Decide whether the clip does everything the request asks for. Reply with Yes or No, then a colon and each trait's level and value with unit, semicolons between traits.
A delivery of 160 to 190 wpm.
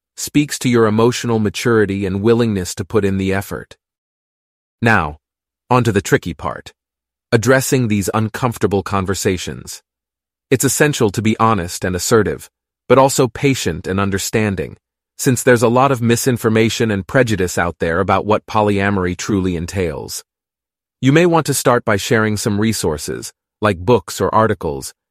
No: average, 150 wpm